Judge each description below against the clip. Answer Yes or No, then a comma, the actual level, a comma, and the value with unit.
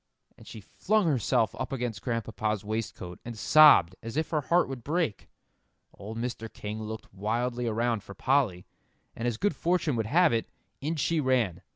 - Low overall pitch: Yes, low, 120 Hz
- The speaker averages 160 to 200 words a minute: Yes, average, 175 wpm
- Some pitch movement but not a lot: Yes, average, 4.9 semitones